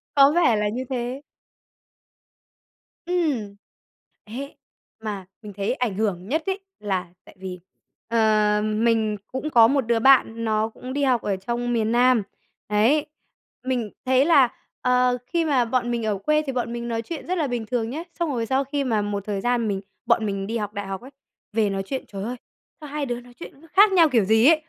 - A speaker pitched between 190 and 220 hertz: No, high, 235 Hz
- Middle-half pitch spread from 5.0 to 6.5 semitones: No, average, 4.0 semitones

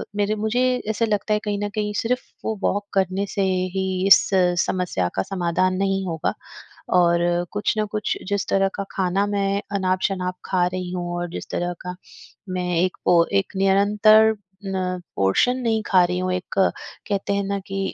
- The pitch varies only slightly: Yes, narrow, 2.3 semitones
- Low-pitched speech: No, high, 195 Hz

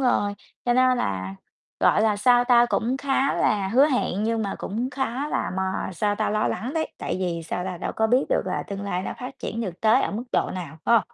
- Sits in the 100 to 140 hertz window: No, high, 220 Hz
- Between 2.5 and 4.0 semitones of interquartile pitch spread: No, average, 4.7 semitones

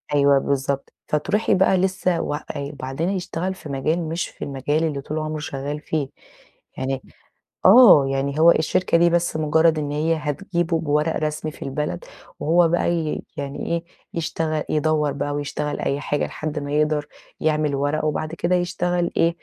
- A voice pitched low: No, medium, 155 Hz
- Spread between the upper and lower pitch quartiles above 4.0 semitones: No, average, 2.7 semitones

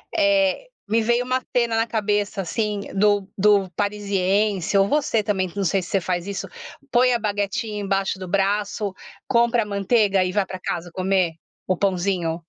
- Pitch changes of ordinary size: No, narrow, 2.3 semitones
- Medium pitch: No, high, 200 Hz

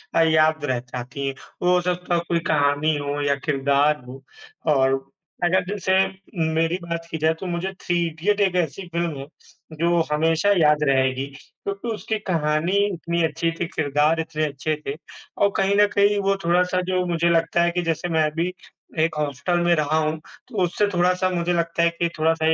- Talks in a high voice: No, medium, 165 Hz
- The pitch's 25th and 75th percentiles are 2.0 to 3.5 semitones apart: Yes, average, 2.8 semitones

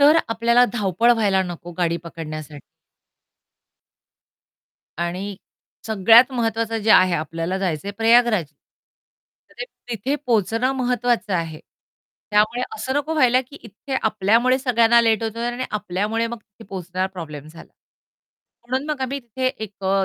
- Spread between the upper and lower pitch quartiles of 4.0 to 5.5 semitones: Yes, average, 4.6 semitones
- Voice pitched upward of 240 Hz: No, high, 220 Hz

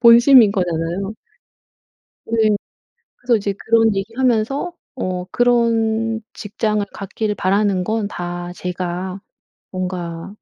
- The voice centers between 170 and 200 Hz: No, high, 210 Hz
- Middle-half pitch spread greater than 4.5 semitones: No, average, 3.6 semitones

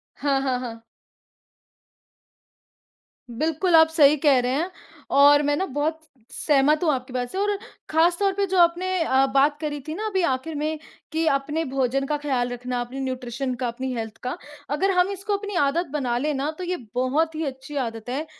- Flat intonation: No, average, 4.0 semitones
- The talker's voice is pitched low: No, very high, 290 Hz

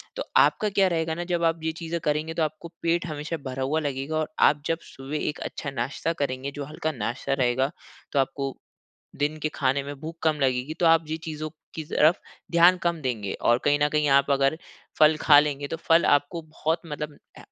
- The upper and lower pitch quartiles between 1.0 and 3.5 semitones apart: Yes, average, 2.8 semitones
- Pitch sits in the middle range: Yes, medium, 150 Hz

